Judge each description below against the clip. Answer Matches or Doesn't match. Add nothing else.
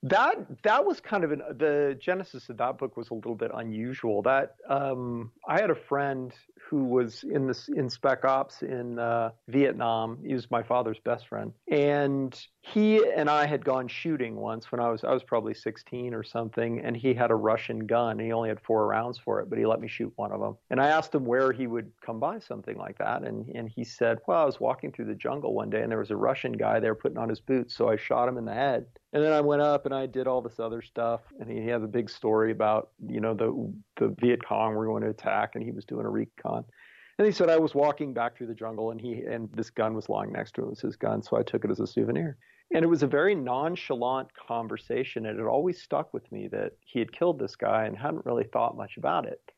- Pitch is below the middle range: Matches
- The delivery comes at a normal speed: Doesn't match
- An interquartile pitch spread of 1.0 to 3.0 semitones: Doesn't match